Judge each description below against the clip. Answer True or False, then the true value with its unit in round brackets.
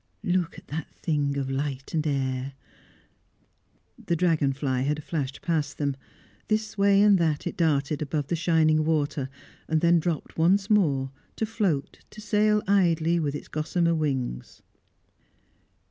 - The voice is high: False (155 Hz)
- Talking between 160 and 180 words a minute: False (145 wpm)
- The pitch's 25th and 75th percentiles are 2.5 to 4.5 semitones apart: True (3.8 semitones)